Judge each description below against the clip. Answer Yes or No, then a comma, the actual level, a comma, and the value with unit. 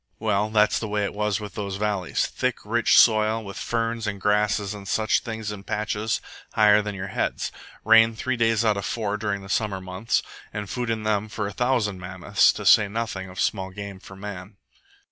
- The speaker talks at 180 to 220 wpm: Yes, average, 200 wpm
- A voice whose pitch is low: Yes, low, 105 Hz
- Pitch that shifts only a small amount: Yes, narrow, 1.9 semitones